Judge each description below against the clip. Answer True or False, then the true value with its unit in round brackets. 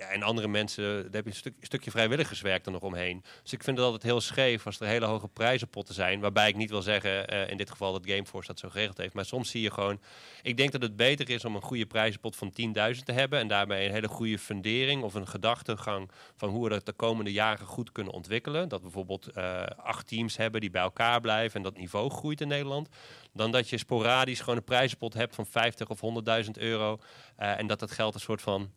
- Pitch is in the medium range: False (110 Hz)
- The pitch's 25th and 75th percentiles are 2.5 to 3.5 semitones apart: True (2.9 semitones)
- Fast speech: True (250 wpm)